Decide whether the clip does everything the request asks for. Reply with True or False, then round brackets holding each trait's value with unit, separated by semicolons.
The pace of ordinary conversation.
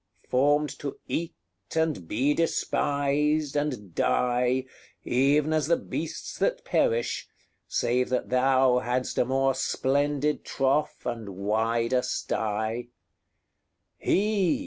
False (105 wpm)